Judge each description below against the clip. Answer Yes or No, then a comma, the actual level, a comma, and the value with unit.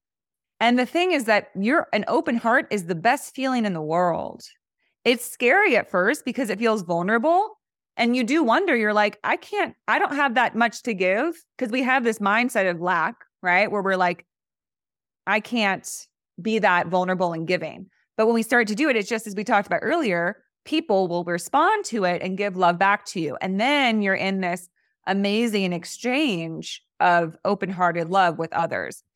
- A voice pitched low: No, high, 210 Hz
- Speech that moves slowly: No, average, 195 wpm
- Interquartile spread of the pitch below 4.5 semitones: No, average, 5.1 semitones